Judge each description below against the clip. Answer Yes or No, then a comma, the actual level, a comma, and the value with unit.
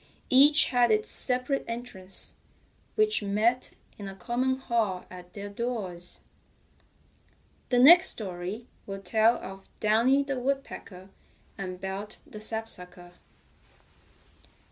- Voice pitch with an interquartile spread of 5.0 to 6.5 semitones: No, average, 4.5 semitones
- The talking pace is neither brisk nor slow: No, slow, 110 wpm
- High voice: Yes, high, 220 Hz